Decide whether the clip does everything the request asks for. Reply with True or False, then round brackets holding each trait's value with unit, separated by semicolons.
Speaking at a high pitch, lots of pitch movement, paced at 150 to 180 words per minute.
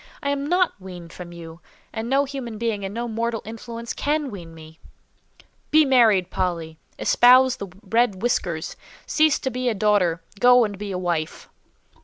True (220 Hz; 5.7 semitones; 170 wpm)